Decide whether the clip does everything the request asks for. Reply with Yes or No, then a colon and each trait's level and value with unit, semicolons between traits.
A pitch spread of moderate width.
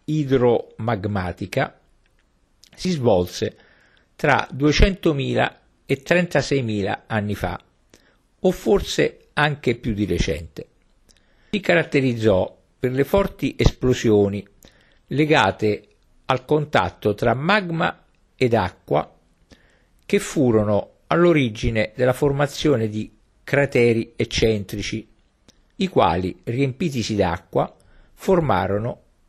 No: wide, 6.3 semitones